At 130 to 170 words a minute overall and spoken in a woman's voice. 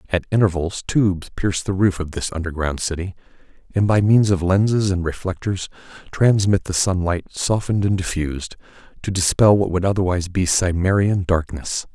No: average, 155 wpm; male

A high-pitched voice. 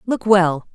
Yes: high, 195 Hz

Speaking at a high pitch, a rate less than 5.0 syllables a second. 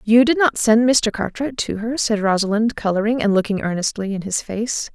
No: high, 220 Hz; 5.2 syllables/s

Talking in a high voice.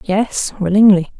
Yes: high, 195 Hz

